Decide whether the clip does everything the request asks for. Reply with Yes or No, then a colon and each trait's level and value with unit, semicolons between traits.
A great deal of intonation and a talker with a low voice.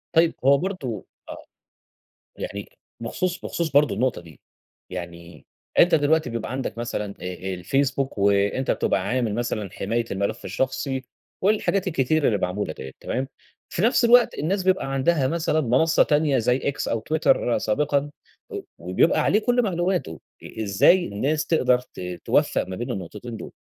Yes: wide, 7.4 semitones; low, 130 Hz